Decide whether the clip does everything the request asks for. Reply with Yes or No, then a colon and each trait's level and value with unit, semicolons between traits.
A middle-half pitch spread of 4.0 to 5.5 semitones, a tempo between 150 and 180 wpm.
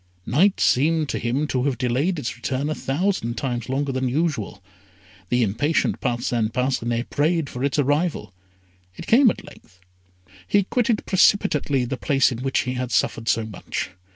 Yes: average, 4.3 semitones; average, 165 wpm